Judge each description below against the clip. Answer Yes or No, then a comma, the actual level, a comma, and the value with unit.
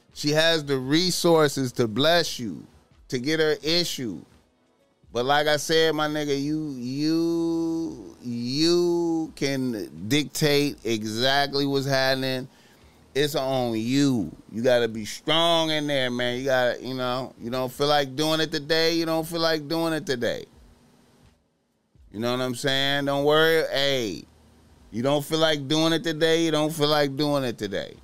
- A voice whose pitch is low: No, medium, 145 Hz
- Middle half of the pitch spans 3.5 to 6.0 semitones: Yes, average, 4.0 semitones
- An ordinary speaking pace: Yes, average, 165 wpm